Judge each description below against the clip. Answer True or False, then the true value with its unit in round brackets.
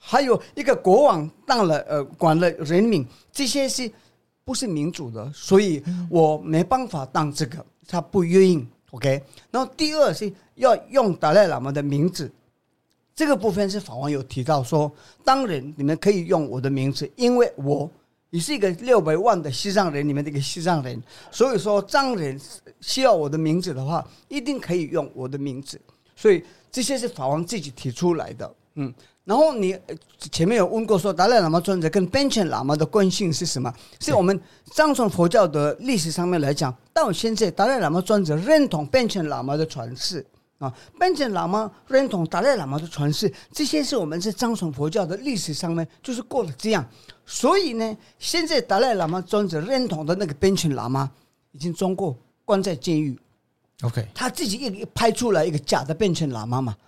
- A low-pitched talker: False (175 Hz)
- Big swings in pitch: True (6.7 semitones)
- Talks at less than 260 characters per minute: False (285 characters per minute)